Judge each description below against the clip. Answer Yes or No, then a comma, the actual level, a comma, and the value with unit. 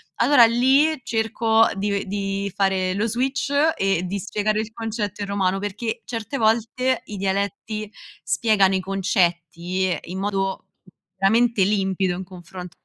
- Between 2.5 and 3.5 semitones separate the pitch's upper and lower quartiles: Yes, average, 2.9 semitones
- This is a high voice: Yes, high, 200 Hz